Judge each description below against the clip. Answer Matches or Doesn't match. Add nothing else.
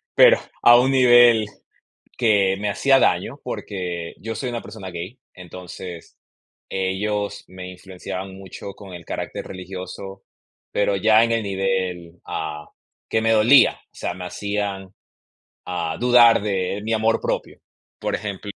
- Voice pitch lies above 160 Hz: Doesn't match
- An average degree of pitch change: Matches